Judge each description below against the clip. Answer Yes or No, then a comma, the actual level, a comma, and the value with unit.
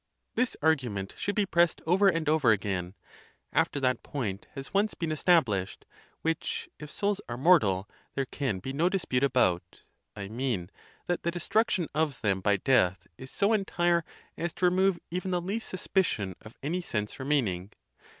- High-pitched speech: No, medium, 145 Hz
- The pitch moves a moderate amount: No, wide, 9.0 semitones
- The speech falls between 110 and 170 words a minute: Yes, average, 165 wpm